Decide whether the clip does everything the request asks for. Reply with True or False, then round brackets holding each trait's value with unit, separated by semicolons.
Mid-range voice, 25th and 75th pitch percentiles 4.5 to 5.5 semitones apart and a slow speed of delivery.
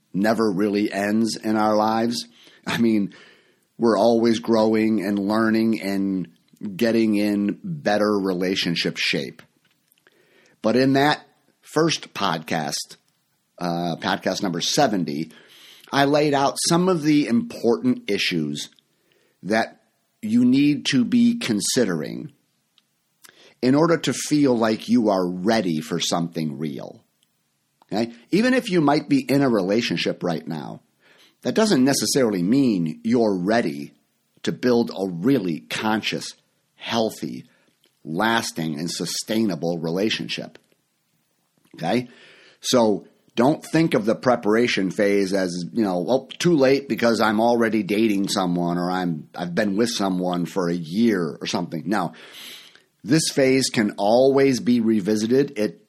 False (110 Hz; 5.2 semitones; 130 wpm)